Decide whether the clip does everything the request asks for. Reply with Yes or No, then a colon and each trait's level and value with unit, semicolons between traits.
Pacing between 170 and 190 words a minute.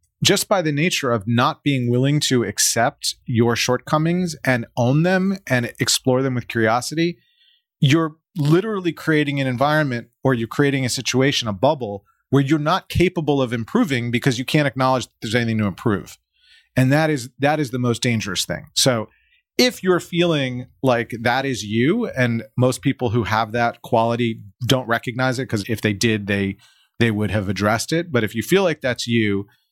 Yes: average, 185 wpm